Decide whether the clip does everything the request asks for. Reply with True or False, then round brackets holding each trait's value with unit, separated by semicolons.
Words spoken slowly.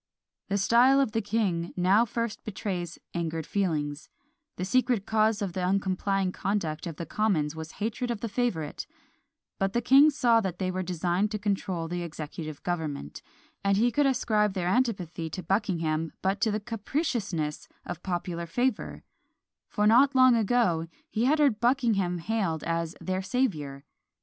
False (160 wpm)